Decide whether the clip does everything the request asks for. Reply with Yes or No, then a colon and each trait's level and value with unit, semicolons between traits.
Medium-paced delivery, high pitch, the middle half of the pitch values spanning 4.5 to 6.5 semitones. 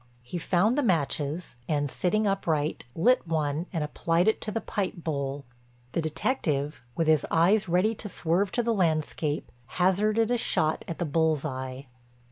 No: average, 165 wpm; medium, 165 Hz; average, 4.9 semitones